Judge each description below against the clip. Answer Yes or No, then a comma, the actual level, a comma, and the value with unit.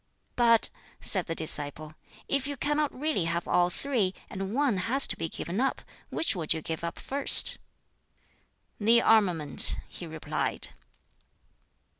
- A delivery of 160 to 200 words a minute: No, average, 140 wpm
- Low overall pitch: No, high, 195 Hz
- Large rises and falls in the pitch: Yes, wide, 8.0 semitones